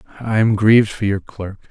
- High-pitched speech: No, low, 105 Hz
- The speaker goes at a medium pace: No, fast, 210 wpm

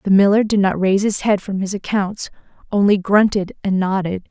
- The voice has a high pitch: Yes, high, 195 Hz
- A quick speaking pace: No, average, 195 wpm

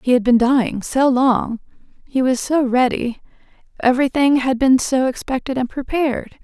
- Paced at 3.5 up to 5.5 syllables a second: Yes, 5.0 syllables/s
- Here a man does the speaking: No, female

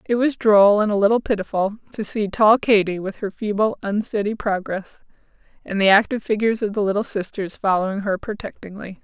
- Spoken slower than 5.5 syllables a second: No, 5.6 syllables/s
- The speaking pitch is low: No, high, 205 Hz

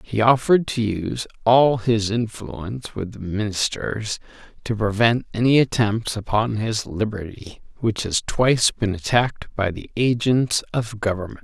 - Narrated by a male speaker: Yes, male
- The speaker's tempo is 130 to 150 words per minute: Yes, average, 140 wpm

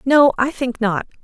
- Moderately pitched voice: No, very high, 250 Hz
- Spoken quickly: No, average, 195 wpm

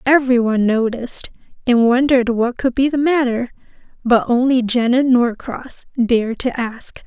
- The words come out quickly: No, average, 145 wpm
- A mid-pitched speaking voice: No, high, 245 Hz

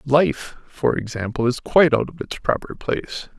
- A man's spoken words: Yes, male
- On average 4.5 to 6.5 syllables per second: Yes, 4.8 syllables/s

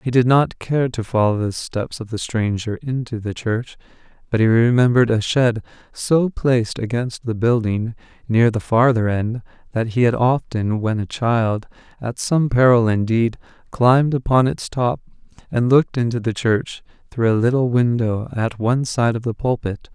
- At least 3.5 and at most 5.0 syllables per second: Yes, 4.6 syllables/s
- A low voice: Yes, low, 120 Hz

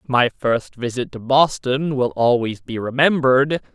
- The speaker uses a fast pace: No, average, 145 wpm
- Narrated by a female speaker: No, male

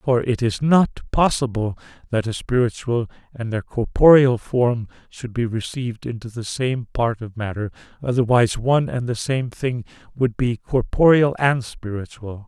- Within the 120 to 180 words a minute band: Yes, average, 155 wpm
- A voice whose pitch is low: Yes, low, 120 Hz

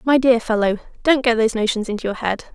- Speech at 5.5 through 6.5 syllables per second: Yes, 6.3 syllables/s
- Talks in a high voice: Yes, high, 235 Hz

